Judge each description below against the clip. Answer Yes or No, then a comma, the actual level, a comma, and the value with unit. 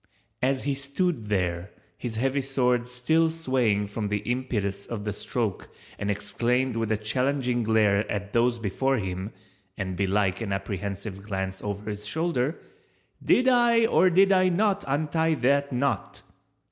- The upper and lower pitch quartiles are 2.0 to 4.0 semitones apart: No, wide, 5.4 semitones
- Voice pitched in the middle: No, low, 120 Hz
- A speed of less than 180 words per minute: Yes, average, 150 wpm